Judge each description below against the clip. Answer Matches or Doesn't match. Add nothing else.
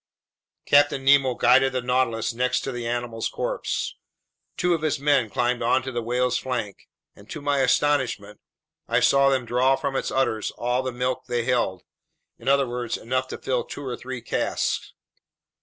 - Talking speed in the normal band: Matches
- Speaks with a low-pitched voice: Matches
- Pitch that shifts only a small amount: Matches